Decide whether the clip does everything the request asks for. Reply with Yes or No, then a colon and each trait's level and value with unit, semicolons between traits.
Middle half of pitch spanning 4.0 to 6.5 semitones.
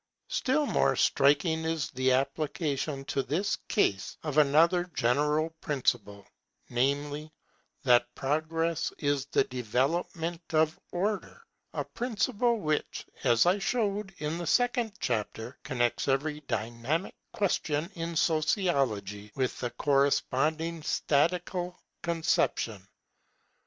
Yes: average, 4.3 semitones